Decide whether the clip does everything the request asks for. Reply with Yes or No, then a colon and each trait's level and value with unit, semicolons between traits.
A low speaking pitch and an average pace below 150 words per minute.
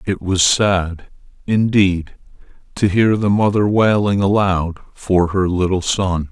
Yes: very low, 95 Hz; slow, 135 wpm